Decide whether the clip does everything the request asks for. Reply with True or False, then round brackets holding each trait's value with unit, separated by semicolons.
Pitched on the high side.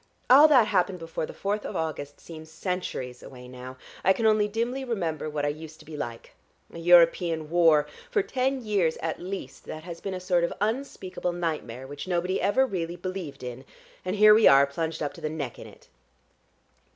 False (170 Hz)